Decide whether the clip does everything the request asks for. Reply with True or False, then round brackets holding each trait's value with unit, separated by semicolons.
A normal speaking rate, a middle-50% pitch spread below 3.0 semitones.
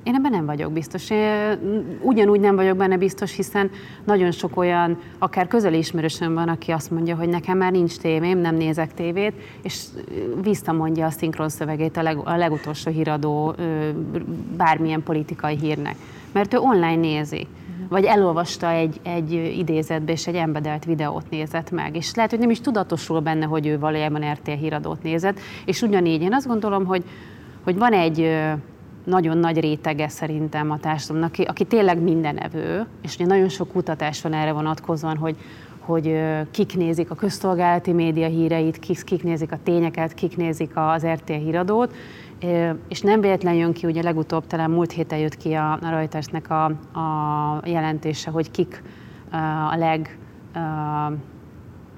False (160 wpm; 2.4 semitones)